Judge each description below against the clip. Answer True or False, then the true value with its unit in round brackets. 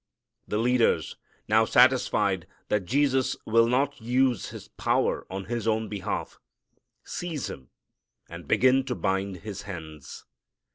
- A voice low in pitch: True (115 Hz)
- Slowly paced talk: True (130 wpm)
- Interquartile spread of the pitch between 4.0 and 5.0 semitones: True (4.7 semitones)